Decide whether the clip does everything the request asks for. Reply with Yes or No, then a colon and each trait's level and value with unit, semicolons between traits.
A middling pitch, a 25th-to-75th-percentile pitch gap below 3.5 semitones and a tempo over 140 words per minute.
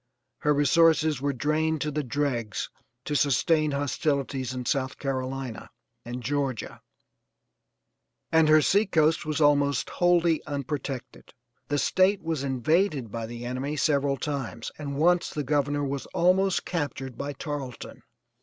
No: medium, 145 Hz; average, 2.7 semitones; slow, 135 wpm